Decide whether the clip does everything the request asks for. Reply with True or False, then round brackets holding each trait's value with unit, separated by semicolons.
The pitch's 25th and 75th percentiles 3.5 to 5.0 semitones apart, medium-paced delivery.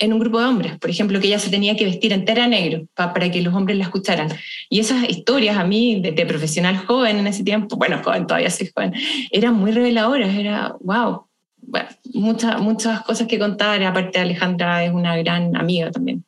False (4.0 semitones; 210 wpm)